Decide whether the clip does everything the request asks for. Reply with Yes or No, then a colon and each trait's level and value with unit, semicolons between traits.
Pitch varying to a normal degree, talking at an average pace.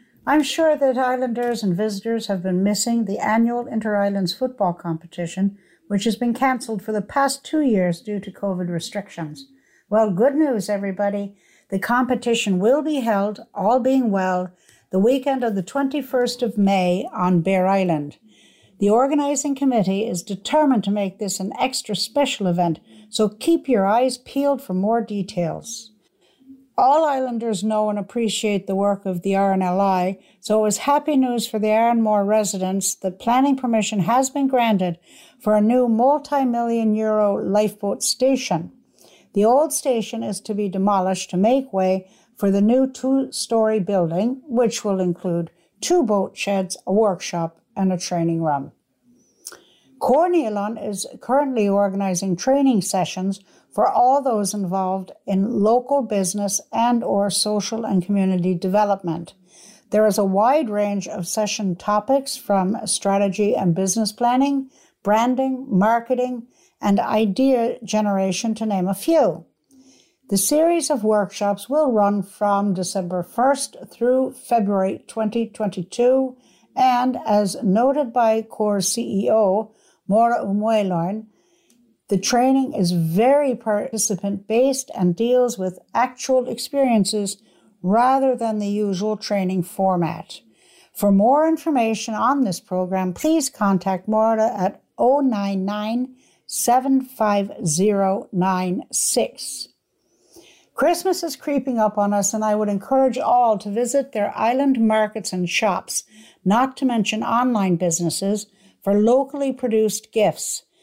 No: average, 4.3 semitones; slow, 130 wpm